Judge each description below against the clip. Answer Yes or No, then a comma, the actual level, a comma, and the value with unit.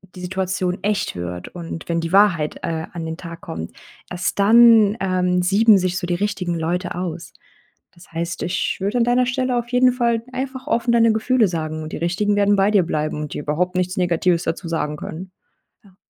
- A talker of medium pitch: Yes, medium, 180 Hz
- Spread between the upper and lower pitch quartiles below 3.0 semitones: No, average, 4.0 semitones